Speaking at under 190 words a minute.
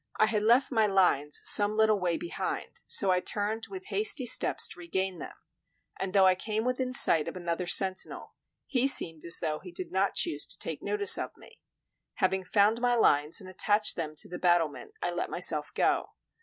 No: average, 195 wpm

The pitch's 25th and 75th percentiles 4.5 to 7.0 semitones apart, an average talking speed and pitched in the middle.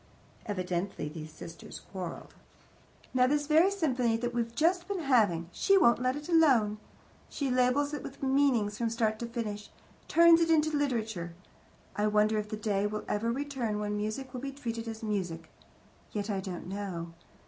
No: average, 5.1 semitones; average, 170 wpm; high, 230 Hz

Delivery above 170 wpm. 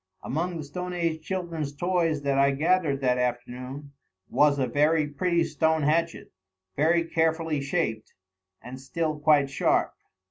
No: average, 140 wpm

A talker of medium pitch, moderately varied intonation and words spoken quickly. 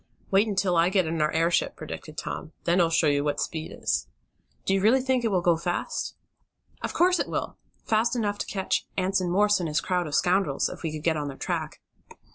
Yes: medium, 180 Hz; average, 4.1 semitones; fast, 225 wpm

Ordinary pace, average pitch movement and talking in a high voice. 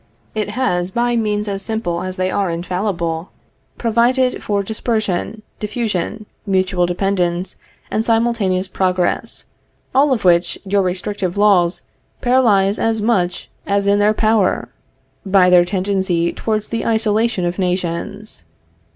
No: slow, 130 wpm; average, 3.2 semitones; high, 200 Hz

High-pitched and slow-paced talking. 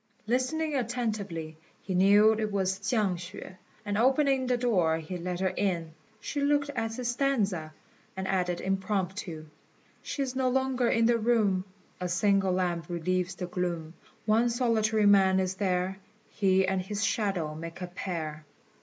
No: high, 195 Hz; average, 155 wpm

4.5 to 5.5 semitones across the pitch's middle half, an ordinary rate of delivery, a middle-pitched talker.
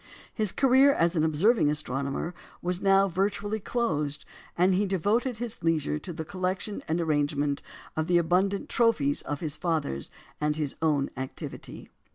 Yes: average, 4.9 semitones; average, 155 wpm; medium, 170 Hz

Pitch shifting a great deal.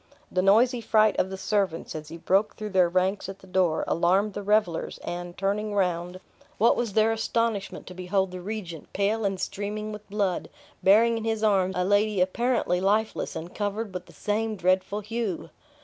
No: average, 2.8 semitones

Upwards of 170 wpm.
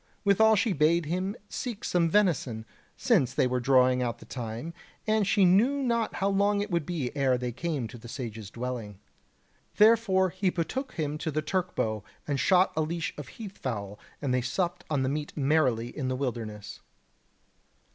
Yes: average, 185 wpm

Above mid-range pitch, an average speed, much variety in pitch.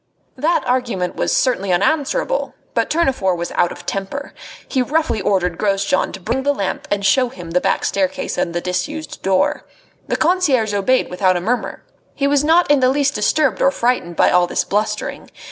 Yes: high, 225 Hz; average, 185 wpm; wide, 6.9 semitones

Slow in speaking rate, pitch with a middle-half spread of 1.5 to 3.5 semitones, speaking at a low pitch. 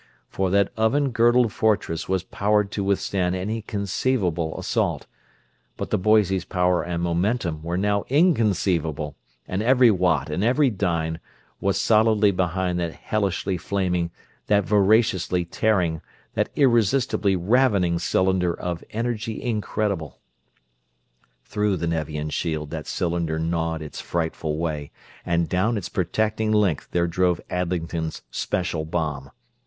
No: slow, 125 wpm; average, 4.0 semitones; very low, 95 Hz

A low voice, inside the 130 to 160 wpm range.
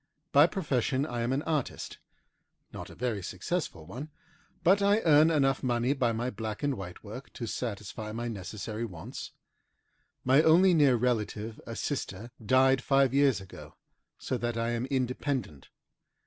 Yes: low, 125 Hz; average, 155 wpm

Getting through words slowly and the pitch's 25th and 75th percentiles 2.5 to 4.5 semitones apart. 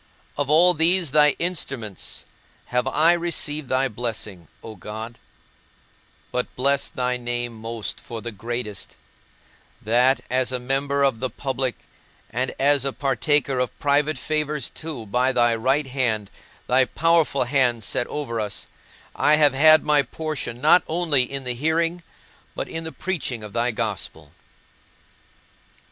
No: average, 145 wpm; average, 3.9 semitones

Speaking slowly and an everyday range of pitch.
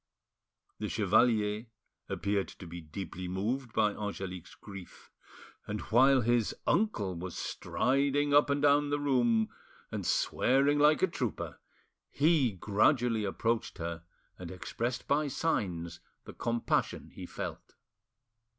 No: slow, 125 wpm; wide, 6.1 semitones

